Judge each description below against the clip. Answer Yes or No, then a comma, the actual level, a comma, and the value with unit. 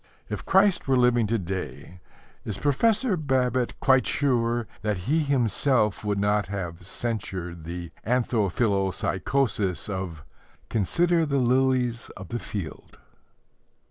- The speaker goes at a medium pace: No, slow, 115 wpm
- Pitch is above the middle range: No, low, 115 Hz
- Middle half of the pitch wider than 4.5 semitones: Yes, wide, 5.6 semitones